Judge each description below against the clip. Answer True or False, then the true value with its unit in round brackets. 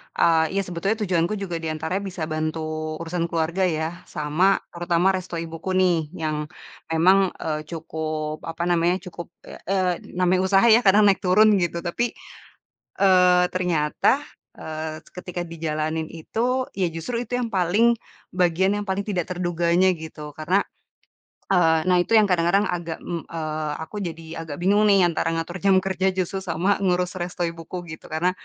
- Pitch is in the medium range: True (175 Hz)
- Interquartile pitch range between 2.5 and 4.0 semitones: True (2.8 semitones)